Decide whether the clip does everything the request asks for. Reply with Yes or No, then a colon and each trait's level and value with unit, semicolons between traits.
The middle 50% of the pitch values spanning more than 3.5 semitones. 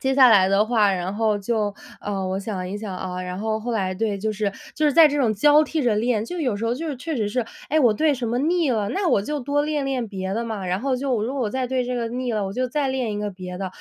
Yes: average, 4.6 semitones